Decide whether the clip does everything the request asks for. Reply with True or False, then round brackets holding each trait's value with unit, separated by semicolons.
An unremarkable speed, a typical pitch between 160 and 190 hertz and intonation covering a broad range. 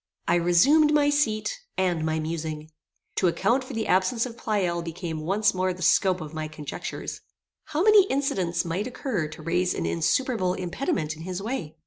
True (175 wpm; 185 Hz; 6.2 semitones)